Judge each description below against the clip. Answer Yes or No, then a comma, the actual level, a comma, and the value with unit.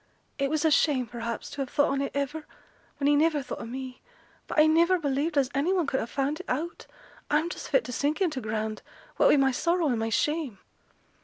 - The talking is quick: Yes, fast, 235 wpm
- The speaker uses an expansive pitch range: No, average, 3.4 semitones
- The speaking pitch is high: Yes, very high, 285 Hz